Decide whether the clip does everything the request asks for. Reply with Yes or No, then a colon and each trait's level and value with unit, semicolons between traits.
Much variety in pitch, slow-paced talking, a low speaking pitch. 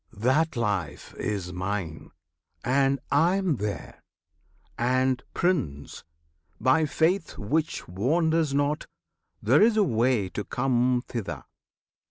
Yes: wide, 7.2 semitones; slow, 110 wpm; low, 130 Hz